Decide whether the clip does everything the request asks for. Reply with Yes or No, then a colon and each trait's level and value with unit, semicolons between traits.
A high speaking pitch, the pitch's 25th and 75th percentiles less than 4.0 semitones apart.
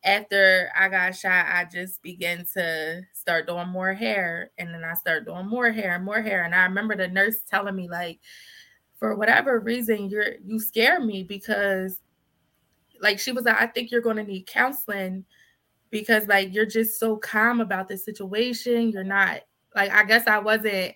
Yes: high, 200 Hz; average, 3.1 semitones